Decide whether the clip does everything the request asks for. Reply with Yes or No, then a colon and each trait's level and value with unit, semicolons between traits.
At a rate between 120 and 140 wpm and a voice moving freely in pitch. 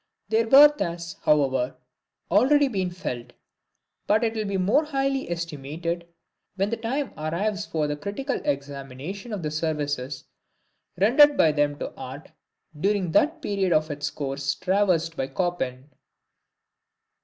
Yes: slow, 135 wpm; wide, 6.4 semitones